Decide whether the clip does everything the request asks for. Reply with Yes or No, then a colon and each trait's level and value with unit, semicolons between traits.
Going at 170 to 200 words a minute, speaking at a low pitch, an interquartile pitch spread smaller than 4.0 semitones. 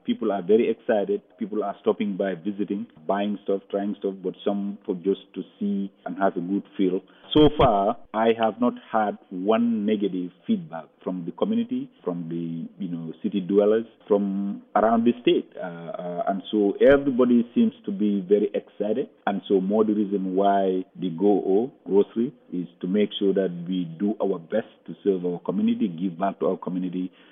Yes: average, 185 wpm; low, 100 Hz; average, 2.9 semitones